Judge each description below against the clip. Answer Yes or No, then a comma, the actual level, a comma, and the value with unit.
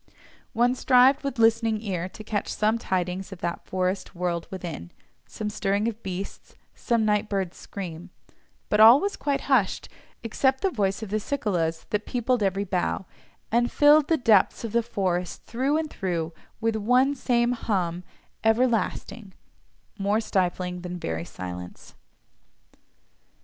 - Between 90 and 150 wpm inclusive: Yes, average, 140 wpm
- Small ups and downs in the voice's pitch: No, average, 4.6 semitones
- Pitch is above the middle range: Yes, high, 210 Hz